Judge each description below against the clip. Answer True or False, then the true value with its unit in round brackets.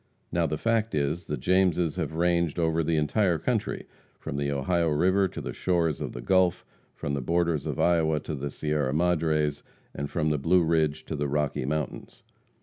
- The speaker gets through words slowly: False (190 wpm)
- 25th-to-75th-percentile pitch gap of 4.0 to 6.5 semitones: False (2.9 semitones)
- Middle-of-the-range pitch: False (80 Hz)